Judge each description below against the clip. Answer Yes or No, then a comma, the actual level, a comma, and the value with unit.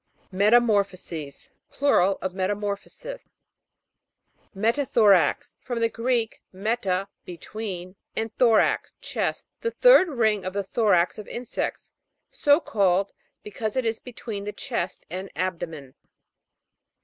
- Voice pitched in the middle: No, high, 210 Hz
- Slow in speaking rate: Yes, slow, 115 wpm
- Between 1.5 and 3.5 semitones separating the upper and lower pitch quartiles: No, average, 4.0 semitones